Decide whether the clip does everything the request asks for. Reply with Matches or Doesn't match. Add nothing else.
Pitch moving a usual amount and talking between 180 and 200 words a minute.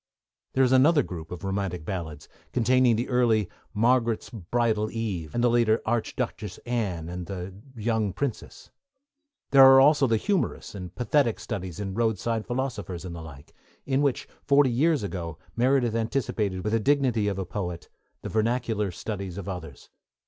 Doesn't match